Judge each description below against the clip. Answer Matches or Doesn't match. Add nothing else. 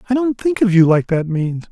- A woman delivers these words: Doesn't match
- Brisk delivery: Matches